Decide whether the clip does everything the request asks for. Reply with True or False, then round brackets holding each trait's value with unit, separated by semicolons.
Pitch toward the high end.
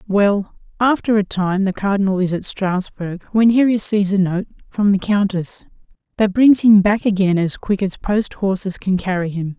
True (195 Hz)